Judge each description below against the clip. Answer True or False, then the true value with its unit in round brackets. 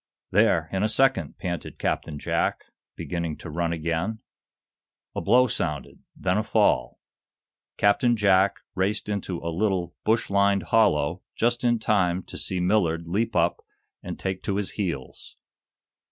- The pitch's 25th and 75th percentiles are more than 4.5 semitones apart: False (3.9 semitones)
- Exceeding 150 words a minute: False (145 wpm)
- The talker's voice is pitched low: True (95 Hz)